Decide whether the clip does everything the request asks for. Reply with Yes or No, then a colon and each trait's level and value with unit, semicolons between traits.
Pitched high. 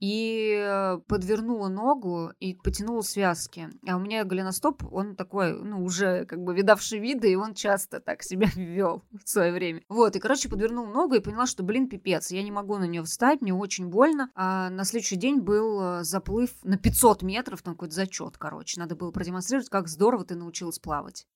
Yes: high, 200 Hz